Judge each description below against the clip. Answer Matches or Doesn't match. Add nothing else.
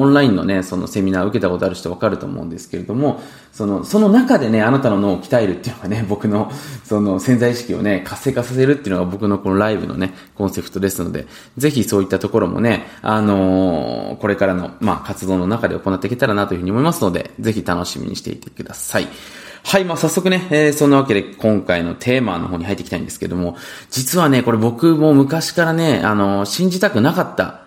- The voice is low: Matches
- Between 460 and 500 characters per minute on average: Matches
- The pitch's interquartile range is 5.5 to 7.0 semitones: Matches